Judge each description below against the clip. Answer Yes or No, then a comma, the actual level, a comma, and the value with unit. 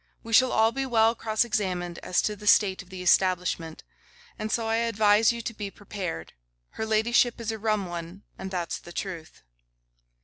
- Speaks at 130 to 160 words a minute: No, average, 190 wpm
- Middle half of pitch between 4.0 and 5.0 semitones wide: No, average, 3.6 semitones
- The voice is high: Yes, high, 210 Hz